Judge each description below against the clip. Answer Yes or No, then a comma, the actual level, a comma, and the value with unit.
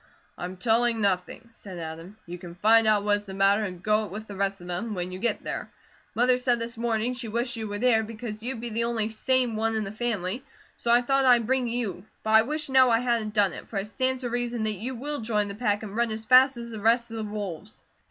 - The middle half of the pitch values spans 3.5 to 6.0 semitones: No, average, 2.8 semitones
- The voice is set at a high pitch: Yes, high, 220 Hz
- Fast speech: Yes, fast, 260 wpm